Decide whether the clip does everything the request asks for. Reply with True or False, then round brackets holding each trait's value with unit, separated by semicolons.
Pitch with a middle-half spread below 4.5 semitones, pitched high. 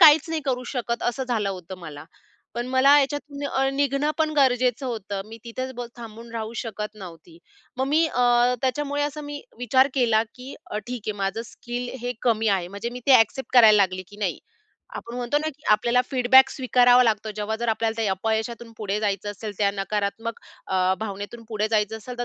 True (3.7 semitones; 235 Hz)